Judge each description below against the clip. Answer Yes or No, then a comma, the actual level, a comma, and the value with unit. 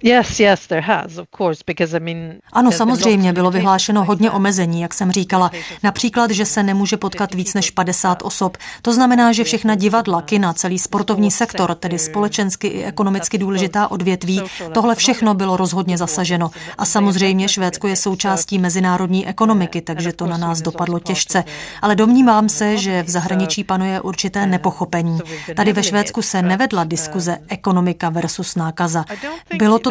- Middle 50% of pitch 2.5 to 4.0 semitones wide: Yes, average, 2.8 semitones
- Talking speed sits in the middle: Yes, average, 140 wpm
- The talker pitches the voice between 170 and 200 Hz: Yes, high, 190 Hz